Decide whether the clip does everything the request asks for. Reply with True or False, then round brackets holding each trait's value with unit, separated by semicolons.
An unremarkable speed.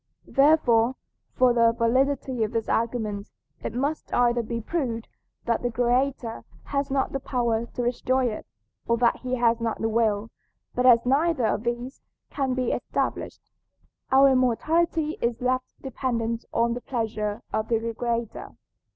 True (150 wpm)